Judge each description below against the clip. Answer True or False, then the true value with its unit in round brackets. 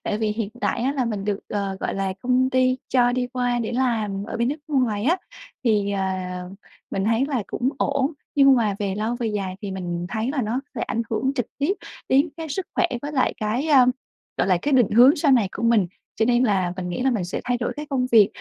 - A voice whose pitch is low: False (235 Hz)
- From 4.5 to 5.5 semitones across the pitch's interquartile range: False (4.0 semitones)